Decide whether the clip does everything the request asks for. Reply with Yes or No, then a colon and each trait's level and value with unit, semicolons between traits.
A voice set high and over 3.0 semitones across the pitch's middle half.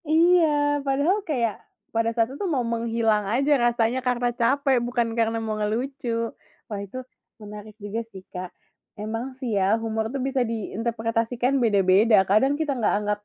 Yes: high, 230 Hz; average, 3.4 semitones